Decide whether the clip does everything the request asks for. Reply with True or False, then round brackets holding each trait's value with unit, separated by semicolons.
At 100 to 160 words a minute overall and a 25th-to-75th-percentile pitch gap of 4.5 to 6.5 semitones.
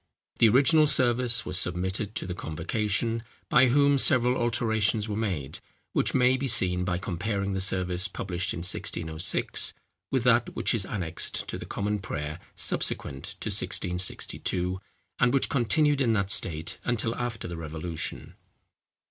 True (150 wpm; 5.2 semitones)